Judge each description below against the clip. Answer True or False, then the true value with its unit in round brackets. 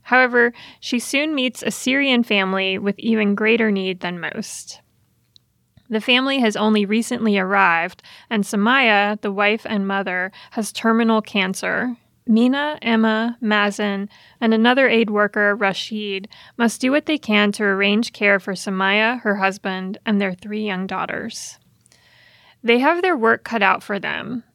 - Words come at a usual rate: True (150 wpm)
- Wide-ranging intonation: False (3.0 semitones)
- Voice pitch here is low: False (215 Hz)